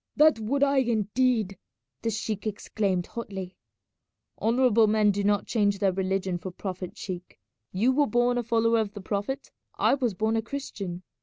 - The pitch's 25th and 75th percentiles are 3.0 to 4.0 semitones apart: Yes, average, 3.6 semitones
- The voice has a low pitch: No, high, 215 Hz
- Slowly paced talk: No, average, 165 wpm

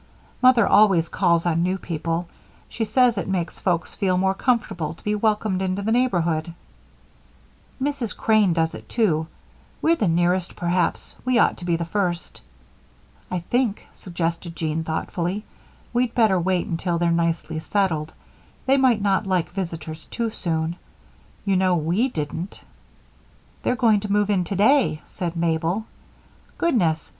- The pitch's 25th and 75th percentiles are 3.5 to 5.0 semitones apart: Yes, average, 4.1 semitones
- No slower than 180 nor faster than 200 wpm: No, average, 150 wpm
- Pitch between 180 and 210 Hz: Yes, medium, 185 Hz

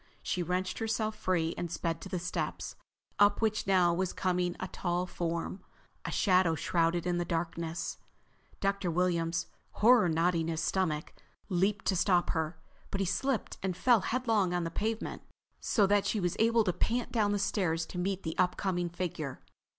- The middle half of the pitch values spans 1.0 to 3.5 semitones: Yes, average, 3.0 semitones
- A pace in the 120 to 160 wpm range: No, average, 175 wpm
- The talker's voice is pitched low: No, medium, 180 Hz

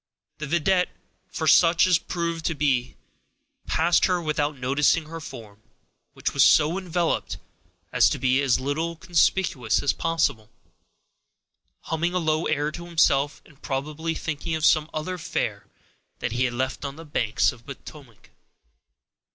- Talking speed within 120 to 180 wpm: Yes, average, 150 wpm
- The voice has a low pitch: No, medium, 155 Hz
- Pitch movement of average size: Yes, average, 3.5 semitones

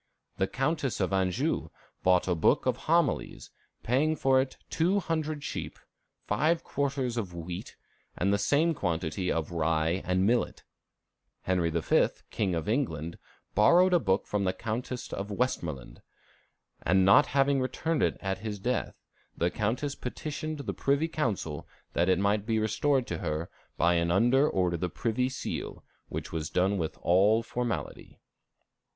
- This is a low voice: Yes, low, 105 Hz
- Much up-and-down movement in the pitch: Yes, wide, 7.1 semitones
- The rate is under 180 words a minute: Yes, average, 155 wpm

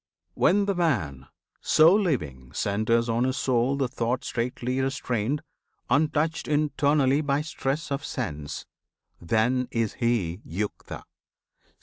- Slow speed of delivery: Yes, slow, 115 wpm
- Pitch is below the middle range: Yes, low, 130 Hz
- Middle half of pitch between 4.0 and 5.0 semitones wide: Yes, average, 4.5 semitones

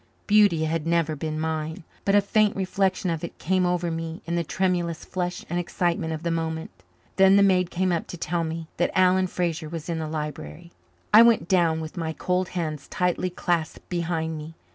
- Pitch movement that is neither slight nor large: No, narrow, 2.2 semitones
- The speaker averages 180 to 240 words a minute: Yes, average, 200 wpm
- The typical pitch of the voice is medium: Yes, medium, 170 Hz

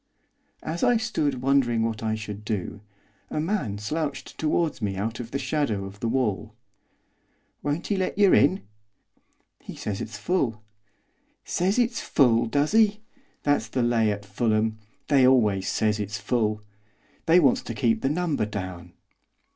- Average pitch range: No, wide, 6.2 semitones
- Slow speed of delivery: No, average, 155 wpm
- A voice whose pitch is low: Yes, low, 120 Hz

